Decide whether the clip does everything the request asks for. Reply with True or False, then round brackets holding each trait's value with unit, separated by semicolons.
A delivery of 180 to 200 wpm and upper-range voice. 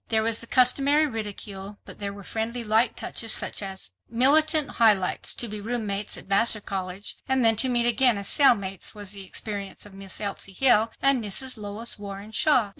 True (185 wpm; 215 Hz)